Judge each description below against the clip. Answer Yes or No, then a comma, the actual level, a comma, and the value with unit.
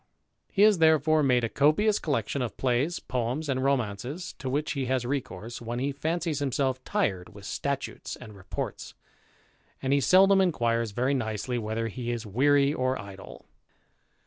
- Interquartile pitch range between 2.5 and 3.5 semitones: No, average, 4.2 semitones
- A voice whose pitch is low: Yes, low, 130 Hz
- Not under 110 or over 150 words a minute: No, average, 160 wpm